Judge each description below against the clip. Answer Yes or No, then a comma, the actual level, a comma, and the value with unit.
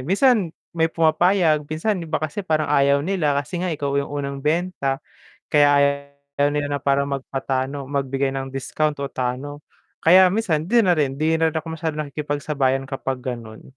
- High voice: No, medium, 145 Hz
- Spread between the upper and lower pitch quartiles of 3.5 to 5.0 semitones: No, average, 2.8 semitones